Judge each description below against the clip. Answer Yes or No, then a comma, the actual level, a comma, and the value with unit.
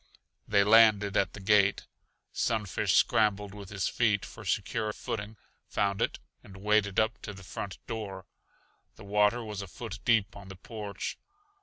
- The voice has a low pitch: Yes, low, 105 Hz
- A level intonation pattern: Yes, narrow, 1.6 semitones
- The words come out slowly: No, average, 160 wpm